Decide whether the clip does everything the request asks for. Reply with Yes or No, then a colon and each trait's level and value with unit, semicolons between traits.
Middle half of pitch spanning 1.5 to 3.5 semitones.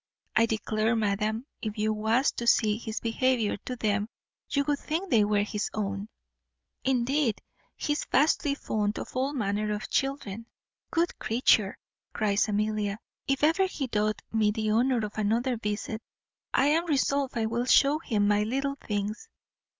No: average, 4.1 semitones